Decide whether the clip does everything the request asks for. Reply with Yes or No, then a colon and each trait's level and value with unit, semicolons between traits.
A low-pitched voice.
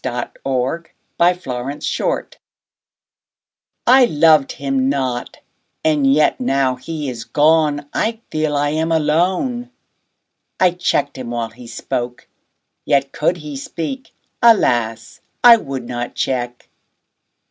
No: medium, 145 Hz